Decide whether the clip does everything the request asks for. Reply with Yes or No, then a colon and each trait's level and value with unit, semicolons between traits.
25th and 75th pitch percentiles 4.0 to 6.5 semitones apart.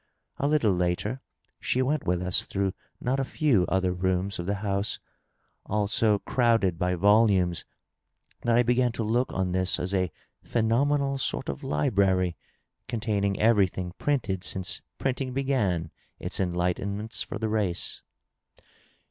Yes: average, 4.5 semitones